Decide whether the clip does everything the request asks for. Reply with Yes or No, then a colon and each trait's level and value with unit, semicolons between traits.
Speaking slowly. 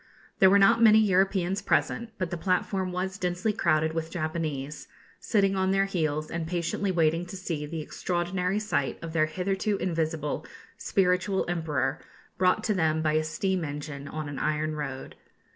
No: average, 165 wpm